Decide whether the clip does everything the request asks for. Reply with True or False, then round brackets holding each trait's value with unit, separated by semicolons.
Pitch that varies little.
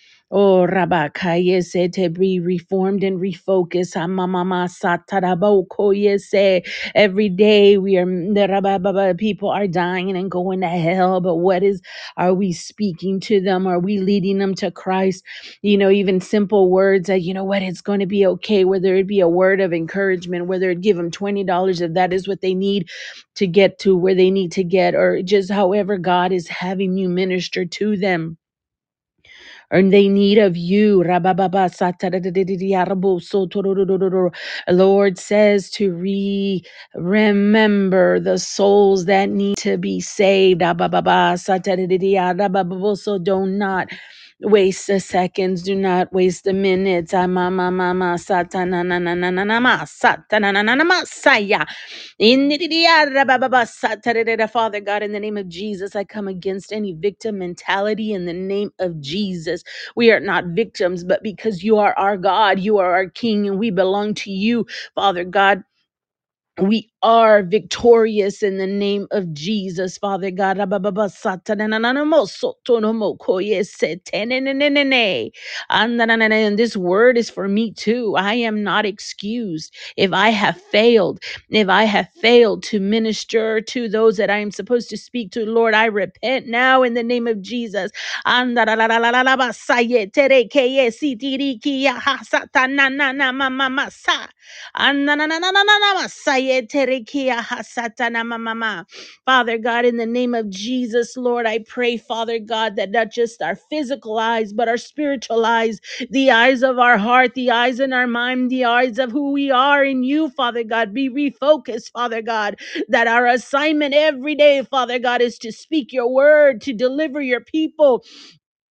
False (3.8 semitones)